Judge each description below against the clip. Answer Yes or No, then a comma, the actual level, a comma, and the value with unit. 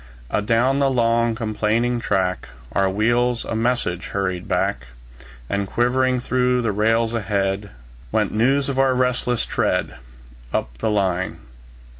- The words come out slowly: Yes, slow, 130 wpm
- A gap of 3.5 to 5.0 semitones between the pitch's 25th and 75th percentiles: Yes, average, 3.8 semitones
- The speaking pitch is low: Yes, low, 115 Hz